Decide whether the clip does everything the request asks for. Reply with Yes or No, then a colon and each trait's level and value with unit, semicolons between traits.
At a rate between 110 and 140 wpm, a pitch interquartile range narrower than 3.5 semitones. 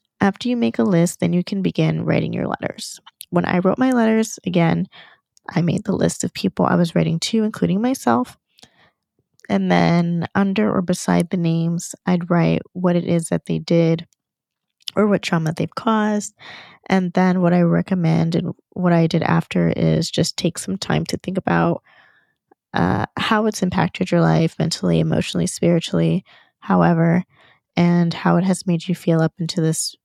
No: average, 175 wpm; narrow, 2.4 semitones